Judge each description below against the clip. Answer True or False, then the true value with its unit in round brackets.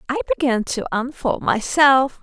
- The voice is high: True (270 Hz)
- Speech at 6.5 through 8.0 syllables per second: False (4.4 syllables/s)